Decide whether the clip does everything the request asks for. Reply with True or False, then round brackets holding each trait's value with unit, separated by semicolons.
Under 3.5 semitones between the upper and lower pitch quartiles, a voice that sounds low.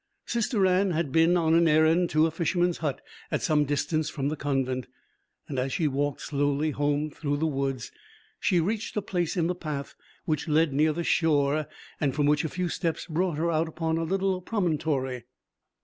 False (3.0 semitones; 155 Hz)